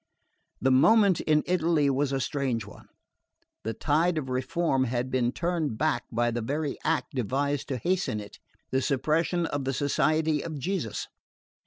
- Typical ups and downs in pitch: Yes, average, 3.8 semitones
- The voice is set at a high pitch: No, medium, 145 Hz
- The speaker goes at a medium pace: Yes, average, 160 wpm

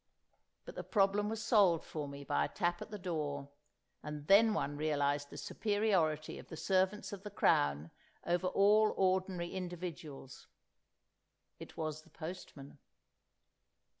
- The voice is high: No, medium, 175 Hz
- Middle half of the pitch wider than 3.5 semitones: Yes, average, 5.1 semitones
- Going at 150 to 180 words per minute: No, average, 140 wpm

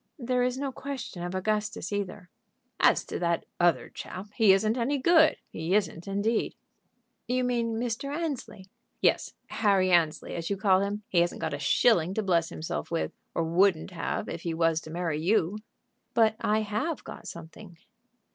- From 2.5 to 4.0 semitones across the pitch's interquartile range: No, average, 5.2 semitones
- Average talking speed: Yes, average, 175 wpm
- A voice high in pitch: Yes, high, 200 Hz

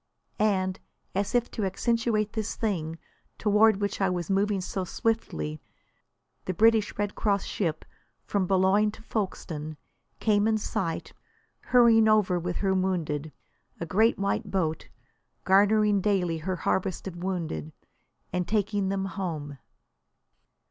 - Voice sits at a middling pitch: No, high, 195 Hz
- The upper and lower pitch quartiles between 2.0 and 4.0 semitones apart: Yes, average, 3.0 semitones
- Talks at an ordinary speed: No, slow, 130 wpm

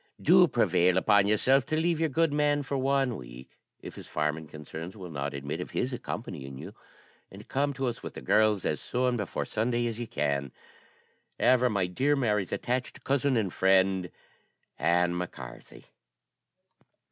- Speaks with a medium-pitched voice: No, low, 105 Hz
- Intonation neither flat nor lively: No, wide, 7.2 semitones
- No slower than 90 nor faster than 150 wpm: No, average, 170 wpm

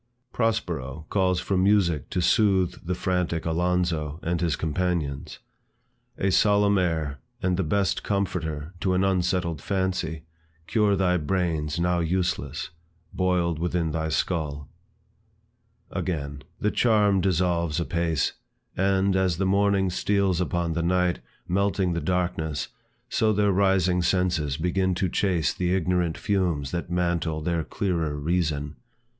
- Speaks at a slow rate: Yes, slow, 130 wpm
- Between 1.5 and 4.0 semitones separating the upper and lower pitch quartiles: Yes, average, 2.7 semitones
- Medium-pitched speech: No, very low, 90 Hz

